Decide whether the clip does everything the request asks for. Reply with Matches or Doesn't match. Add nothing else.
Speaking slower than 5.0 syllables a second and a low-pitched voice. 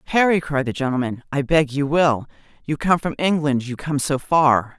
Doesn't match